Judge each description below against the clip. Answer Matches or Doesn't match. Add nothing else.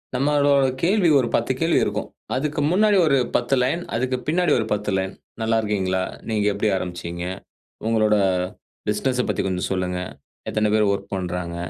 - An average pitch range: Doesn't match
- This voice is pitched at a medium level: Doesn't match